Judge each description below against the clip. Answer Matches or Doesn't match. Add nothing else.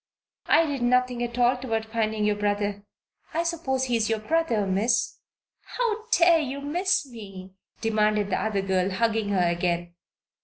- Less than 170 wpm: Matches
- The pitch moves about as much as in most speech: Matches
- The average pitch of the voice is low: Doesn't match